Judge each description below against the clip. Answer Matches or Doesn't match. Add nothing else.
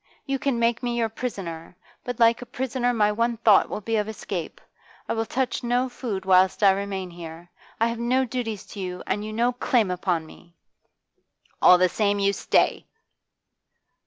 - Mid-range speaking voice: Doesn't match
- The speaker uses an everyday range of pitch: Matches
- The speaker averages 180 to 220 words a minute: Matches